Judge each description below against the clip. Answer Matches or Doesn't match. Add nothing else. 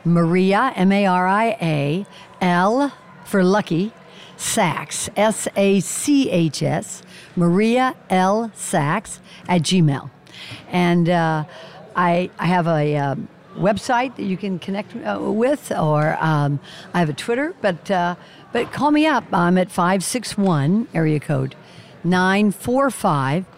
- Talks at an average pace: Doesn't match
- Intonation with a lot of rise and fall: Doesn't match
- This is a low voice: Doesn't match